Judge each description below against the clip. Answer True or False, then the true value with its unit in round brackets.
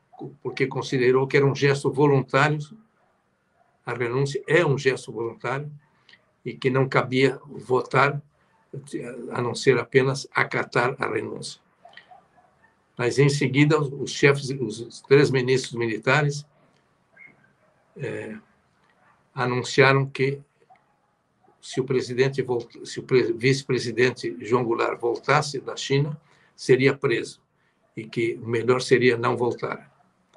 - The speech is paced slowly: True (110 wpm)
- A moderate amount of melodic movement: False (2.1 semitones)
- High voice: False (135 Hz)